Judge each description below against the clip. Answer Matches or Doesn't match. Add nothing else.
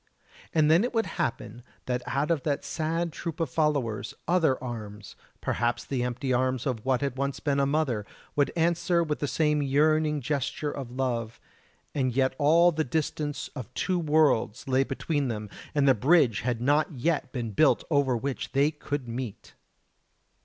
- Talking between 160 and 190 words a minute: Matches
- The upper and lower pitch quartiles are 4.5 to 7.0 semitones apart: Doesn't match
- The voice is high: Doesn't match